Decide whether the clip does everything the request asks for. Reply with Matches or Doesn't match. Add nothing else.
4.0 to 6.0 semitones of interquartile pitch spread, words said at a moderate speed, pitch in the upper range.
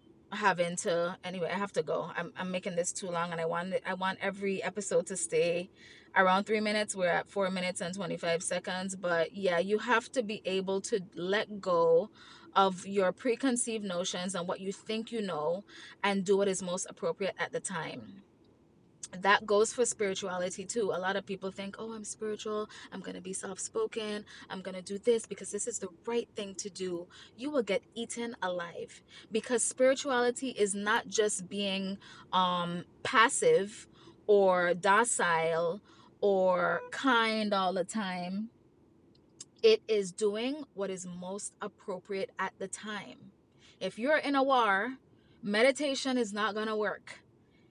Doesn't match